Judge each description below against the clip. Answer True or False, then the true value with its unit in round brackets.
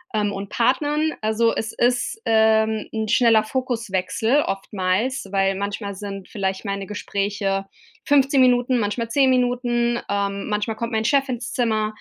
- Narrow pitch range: False (3.5 semitones)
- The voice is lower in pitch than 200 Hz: False (220 Hz)